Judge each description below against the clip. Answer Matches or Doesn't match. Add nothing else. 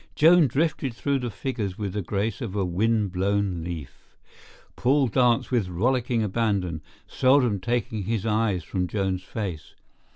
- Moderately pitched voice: Doesn't match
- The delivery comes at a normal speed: Matches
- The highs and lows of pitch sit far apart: Doesn't match